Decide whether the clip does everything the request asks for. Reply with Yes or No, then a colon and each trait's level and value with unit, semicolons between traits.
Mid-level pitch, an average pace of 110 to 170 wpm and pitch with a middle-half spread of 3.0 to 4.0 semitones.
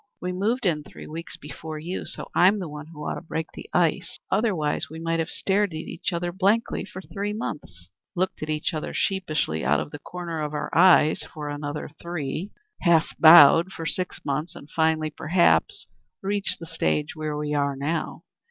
No: medium, 160 Hz; average, 190 wpm; average, 3.3 semitones